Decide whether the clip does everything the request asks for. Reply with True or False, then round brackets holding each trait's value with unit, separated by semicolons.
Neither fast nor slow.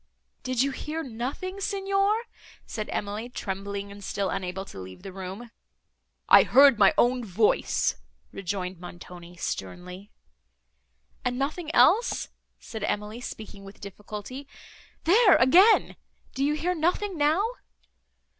False (120 wpm)